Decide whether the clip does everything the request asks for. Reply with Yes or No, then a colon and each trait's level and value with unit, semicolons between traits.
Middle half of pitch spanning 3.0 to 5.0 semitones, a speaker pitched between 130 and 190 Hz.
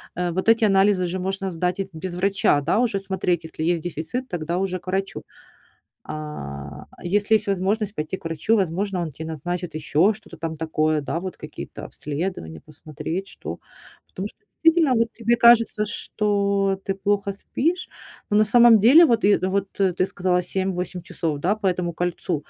Yes: average, 3.7 semitones; medium, 185 Hz